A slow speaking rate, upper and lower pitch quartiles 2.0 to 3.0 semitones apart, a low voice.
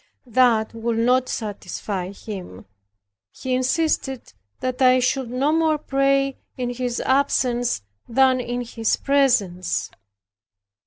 No: slow, 110 wpm; average, 2.7 semitones; very high, 250 Hz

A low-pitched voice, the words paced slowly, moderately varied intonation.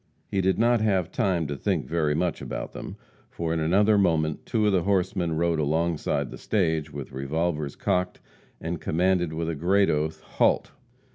No: very low, 85 Hz; average, 180 wpm; average, 3.2 semitones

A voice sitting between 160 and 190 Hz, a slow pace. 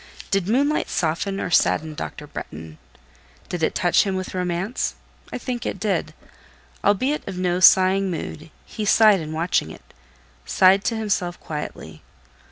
No: medium, 185 Hz; average, 150 wpm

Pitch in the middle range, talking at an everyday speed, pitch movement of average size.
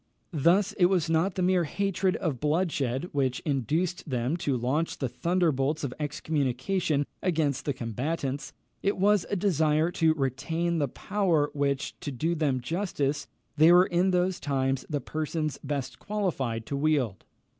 Yes: medium, 155 Hz; average, 155 wpm; average, 4.4 semitones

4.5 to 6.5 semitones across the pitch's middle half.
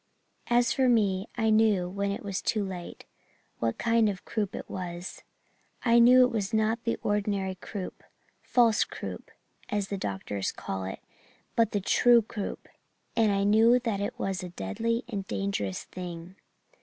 No: average, 3.5 semitones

